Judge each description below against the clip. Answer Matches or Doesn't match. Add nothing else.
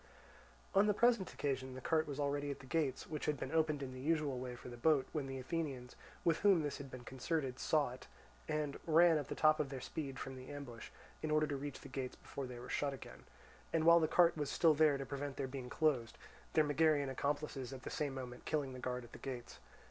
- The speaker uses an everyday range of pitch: Matches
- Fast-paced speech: Matches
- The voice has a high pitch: Doesn't match